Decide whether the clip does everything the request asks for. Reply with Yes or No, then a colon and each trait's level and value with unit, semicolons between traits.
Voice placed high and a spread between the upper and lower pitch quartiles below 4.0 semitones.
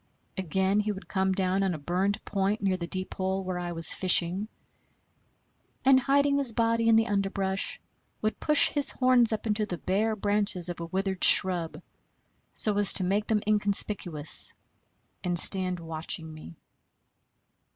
Yes: high, 195 Hz; average, 2.9 semitones